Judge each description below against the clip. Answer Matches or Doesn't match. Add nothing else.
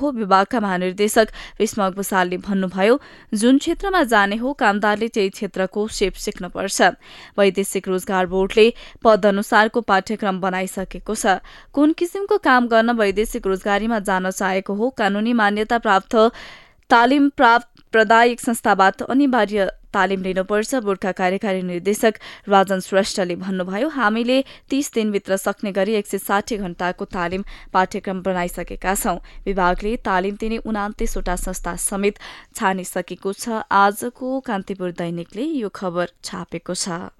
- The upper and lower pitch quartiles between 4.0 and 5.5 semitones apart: Doesn't match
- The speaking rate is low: Matches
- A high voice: Matches